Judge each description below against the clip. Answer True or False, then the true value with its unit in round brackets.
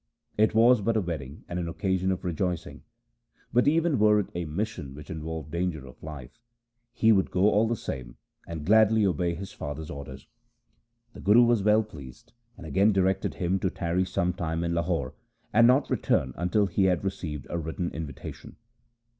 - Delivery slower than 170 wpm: False (185 wpm)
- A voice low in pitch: True (90 Hz)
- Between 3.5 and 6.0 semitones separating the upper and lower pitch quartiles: True (4.7 semitones)